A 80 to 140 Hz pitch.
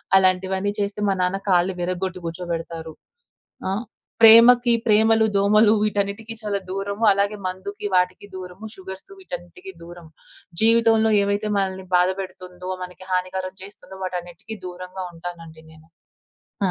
No: high, 190 Hz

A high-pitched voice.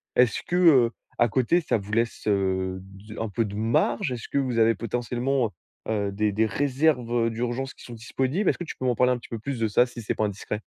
No: low, 115 Hz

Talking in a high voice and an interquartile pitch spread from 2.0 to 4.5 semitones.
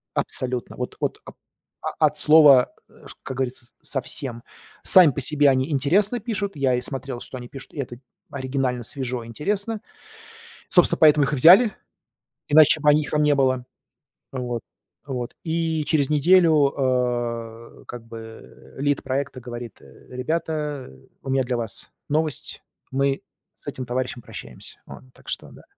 No: low, 135 Hz; average, 3.3 semitones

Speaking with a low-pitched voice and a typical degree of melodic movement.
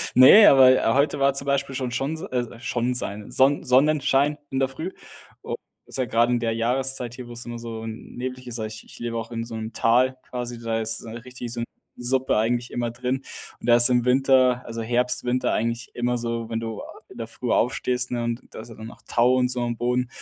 No: low, 120 Hz; narrow, 1.8 semitones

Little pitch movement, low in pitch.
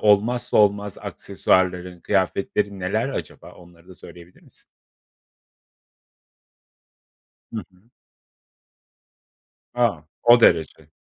No: average, 3.2 semitones; low, 100 Hz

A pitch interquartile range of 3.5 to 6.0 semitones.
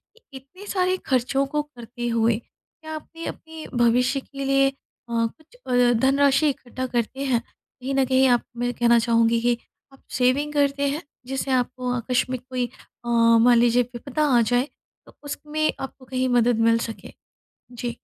No: narrow, 2.6 semitones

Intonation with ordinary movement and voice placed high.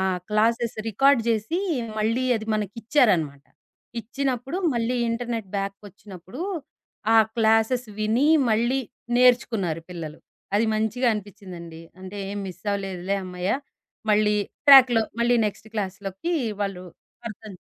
Yes: average, 3.6 semitones; high, 215 Hz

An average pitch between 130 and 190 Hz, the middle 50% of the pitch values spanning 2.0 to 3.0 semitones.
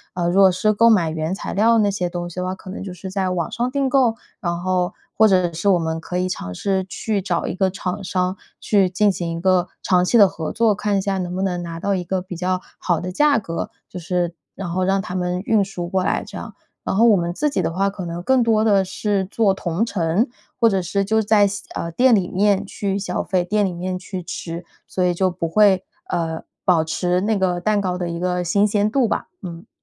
Yes: medium, 185 Hz; narrow, 2.4 semitones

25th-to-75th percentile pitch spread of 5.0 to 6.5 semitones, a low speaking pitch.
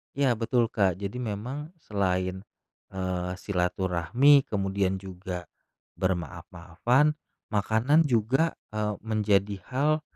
Yes: average, 5.3 semitones; low, 105 Hz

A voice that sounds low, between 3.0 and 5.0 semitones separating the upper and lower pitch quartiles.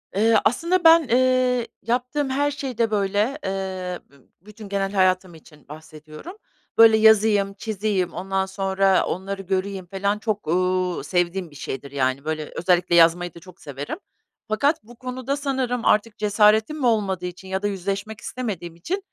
No: high, 195 Hz; average, 4.2 semitones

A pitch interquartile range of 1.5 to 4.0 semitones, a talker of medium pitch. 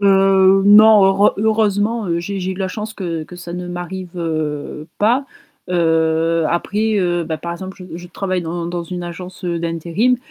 Yes: average, 2.8 semitones; medium, 180 Hz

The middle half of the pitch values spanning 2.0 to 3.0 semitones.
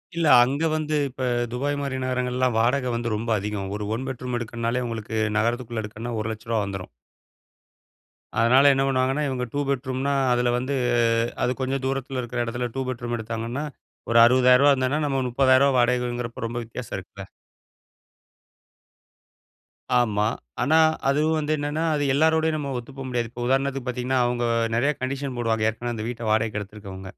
Yes: narrow, 2.6 semitones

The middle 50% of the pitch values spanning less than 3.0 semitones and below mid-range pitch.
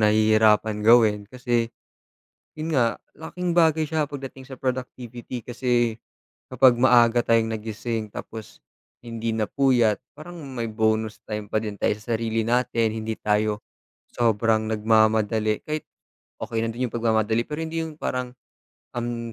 Yes: narrow, 2.6 semitones; low, 115 Hz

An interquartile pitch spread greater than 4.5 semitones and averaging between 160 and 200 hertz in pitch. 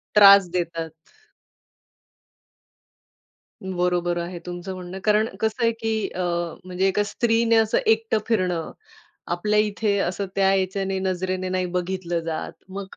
No: average, 2.8 semitones; high, 190 Hz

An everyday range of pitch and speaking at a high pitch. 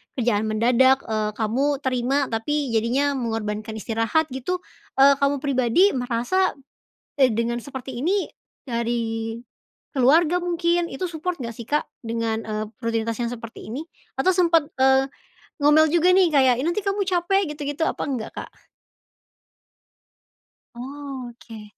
Yes: average, 4.6 semitones; very high, 260 Hz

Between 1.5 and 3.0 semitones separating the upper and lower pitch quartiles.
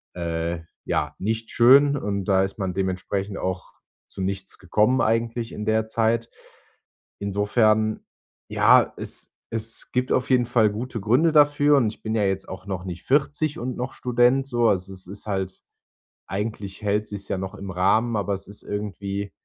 No: average, 3.5 semitones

